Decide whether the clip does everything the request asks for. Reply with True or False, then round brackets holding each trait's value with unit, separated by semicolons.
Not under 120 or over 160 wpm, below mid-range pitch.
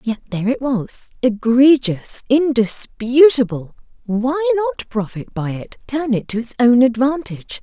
False (135 wpm; 250 Hz)